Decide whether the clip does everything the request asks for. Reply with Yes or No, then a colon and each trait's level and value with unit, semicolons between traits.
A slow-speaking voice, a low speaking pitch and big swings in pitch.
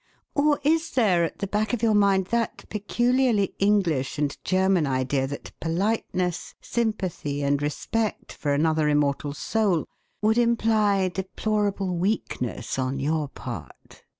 No: slow, 130 wpm; high, 190 Hz; wide, 6.5 semitones